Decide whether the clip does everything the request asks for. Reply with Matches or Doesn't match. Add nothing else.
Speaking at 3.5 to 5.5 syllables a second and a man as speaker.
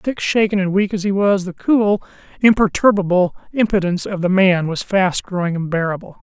Matches